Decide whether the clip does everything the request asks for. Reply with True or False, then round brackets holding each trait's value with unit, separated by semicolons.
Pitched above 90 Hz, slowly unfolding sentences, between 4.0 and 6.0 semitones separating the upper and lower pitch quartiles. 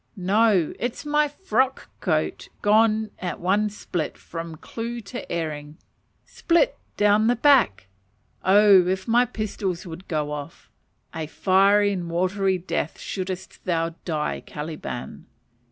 True (190 Hz; 130 wpm; 4.6 semitones)